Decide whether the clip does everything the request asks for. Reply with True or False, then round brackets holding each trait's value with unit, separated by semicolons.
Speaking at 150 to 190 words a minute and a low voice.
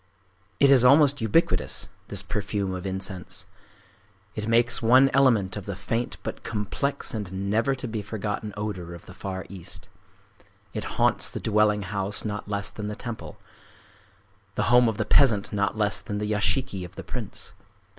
True (160 wpm; 105 Hz)